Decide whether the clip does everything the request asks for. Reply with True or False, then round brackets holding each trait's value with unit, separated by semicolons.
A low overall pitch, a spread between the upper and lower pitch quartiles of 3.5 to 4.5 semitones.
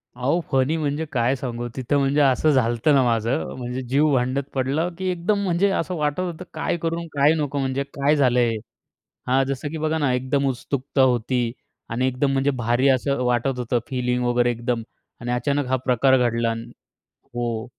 False (130 Hz; 2.8 semitones)